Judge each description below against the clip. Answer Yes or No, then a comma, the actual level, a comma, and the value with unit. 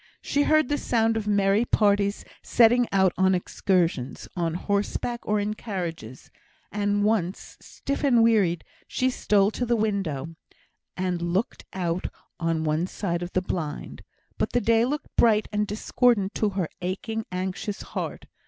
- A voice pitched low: No, high, 200 Hz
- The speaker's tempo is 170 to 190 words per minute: No, average, 155 wpm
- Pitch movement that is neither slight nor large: Yes, average, 3.8 semitones